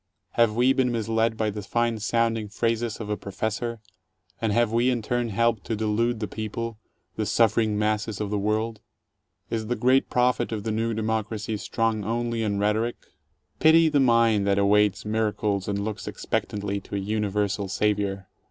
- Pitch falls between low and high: No, low, 110 Hz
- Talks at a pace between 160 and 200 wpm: Yes, average, 170 wpm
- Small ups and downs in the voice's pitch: Yes, narrow, 1.9 semitones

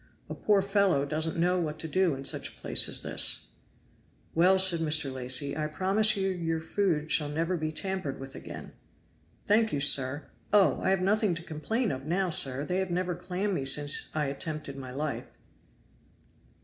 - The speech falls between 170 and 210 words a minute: Yes, average, 185 wpm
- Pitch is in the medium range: Yes, medium, 165 Hz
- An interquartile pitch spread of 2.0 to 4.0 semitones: No, average, 4.4 semitones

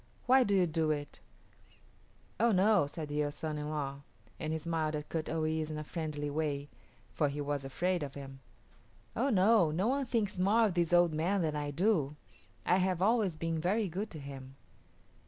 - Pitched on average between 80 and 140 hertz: No, medium, 160 Hz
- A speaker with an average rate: Yes, average, 195 wpm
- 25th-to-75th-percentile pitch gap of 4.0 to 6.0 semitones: Yes, average, 4.4 semitones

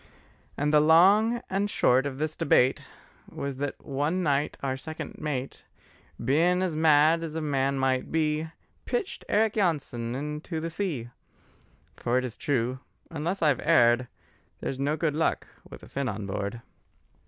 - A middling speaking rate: Yes, average, 155 wpm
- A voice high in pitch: No, medium, 150 Hz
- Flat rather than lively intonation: No, average, 3.7 semitones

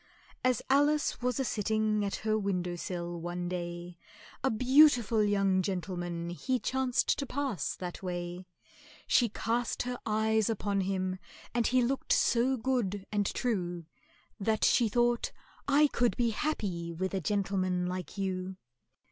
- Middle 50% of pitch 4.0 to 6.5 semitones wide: Yes, average, 4.9 semitones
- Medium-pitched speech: No, high, 205 Hz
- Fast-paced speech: No, average, 145 wpm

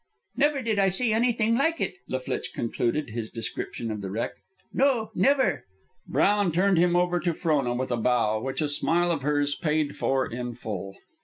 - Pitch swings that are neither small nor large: No, wide, 8.9 semitones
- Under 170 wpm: No, average, 185 wpm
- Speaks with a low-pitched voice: No, medium, 155 Hz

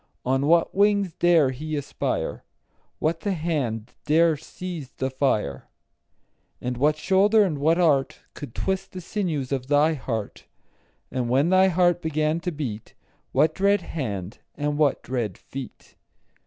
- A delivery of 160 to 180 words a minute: No, average, 150 wpm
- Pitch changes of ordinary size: Yes, average, 4.9 semitones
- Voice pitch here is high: No, medium, 155 Hz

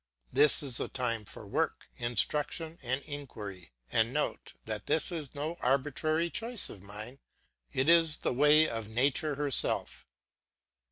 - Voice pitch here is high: No, medium, 140 Hz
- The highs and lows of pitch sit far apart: No, average, 4.7 semitones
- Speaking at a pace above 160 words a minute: No, average, 145 wpm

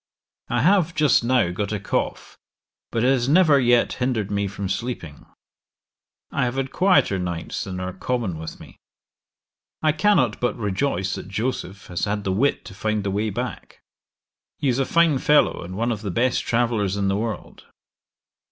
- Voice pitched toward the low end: Yes, low, 115 Hz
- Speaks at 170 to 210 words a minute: Yes, average, 180 wpm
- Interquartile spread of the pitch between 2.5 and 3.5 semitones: No, average, 5.0 semitones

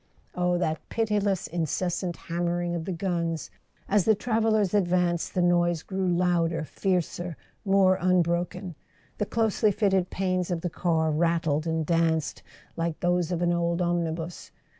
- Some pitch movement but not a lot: No, narrow, 1.9 semitones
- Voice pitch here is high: No, medium, 175 Hz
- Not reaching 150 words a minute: Yes, average, 140 wpm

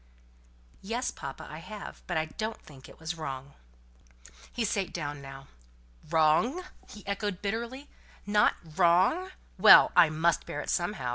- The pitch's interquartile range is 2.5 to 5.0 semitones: No, wide, 5.5 semitones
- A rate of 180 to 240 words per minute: No, average, 145 wpm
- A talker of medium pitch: Yes, medium, 175 Hz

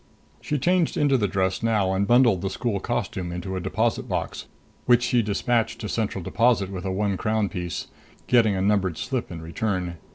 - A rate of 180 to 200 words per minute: Yes, average, 190 wpm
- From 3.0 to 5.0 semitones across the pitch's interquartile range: Yes, average, 3.9 semitones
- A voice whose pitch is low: Yes, low, 105 Hz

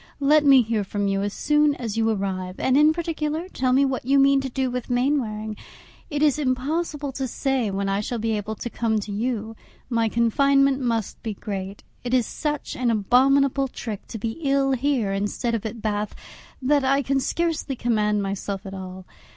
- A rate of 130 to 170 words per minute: No, average, 195 wpm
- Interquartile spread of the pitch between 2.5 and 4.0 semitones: No, average, 4.6 semitones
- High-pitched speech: Yes, high, 245 Hz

